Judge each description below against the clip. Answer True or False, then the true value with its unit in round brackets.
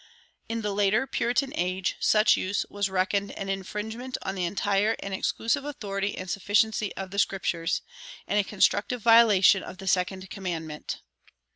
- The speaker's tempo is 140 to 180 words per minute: True (155 wpm)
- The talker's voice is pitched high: True (200 Hz)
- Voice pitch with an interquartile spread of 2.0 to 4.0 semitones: True (2.4 semitones)